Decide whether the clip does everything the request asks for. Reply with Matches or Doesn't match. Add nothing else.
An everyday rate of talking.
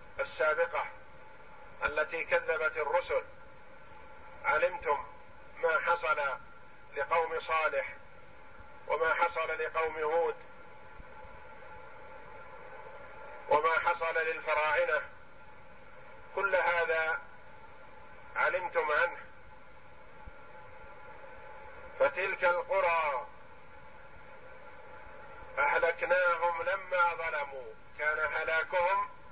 Doesn't match